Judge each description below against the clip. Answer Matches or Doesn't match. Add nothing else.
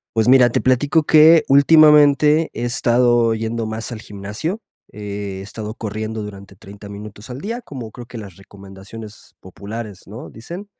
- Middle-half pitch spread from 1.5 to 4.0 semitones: Doesn't match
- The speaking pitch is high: Doesn't match